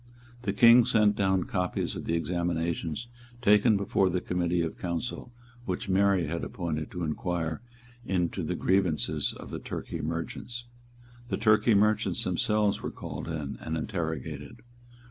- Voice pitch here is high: No, very low, 90 Hz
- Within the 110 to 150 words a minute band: Yes, average, 145 wpm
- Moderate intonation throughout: Yes, average, 3.8 semitones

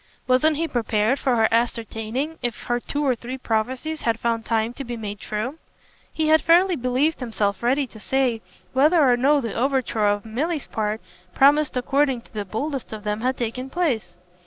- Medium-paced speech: Yes, average, 185 wpm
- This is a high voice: Yes, high, 245 Hz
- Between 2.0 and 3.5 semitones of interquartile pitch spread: No, average, 4.1 semitones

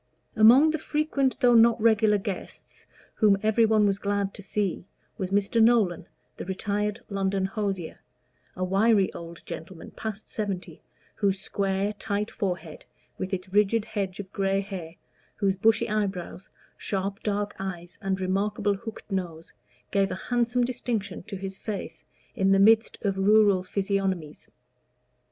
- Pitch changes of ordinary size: No, narrow, 2.2 semitones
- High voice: Yes, high, 200 Hz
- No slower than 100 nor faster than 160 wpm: Yes, average, 145 wpm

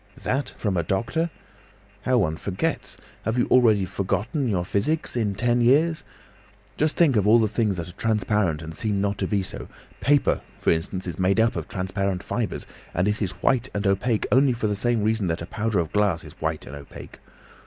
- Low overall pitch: Yes, low, 105 Hz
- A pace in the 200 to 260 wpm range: Yes, fast, 205 wpm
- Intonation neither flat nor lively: Yes, average, 4.2 semitones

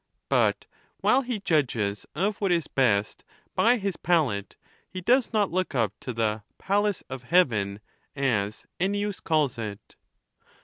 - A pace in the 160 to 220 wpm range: No, average, 145 wpm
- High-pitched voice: No, medium, 155 Hz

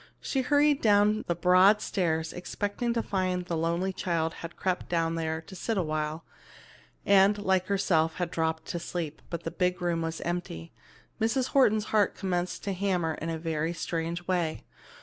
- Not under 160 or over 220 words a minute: Yes, average, 175 wpm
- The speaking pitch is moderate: Yes, medium, 175 Hz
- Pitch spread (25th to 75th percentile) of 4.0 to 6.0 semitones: No, average, 3.4 semitones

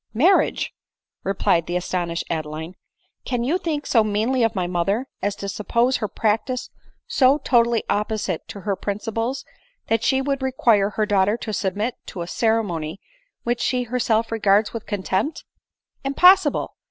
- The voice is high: Yes, high, 220 Hz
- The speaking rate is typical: Yes, average, 155 wpm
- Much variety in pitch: No, average, 4.1 semitones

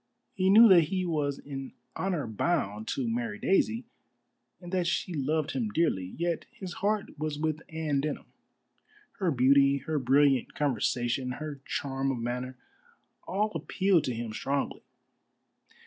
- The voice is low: No, medium, 145 Hz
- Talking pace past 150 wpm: No, average, 145 wpm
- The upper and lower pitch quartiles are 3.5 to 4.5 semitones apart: No, average, 5.2 semitones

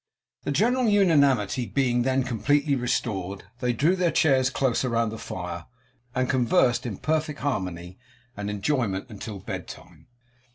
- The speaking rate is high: No, average, 140 wpm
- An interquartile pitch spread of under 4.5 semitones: No, wide, 5.5 semitones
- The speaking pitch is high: No, low, 125 Hz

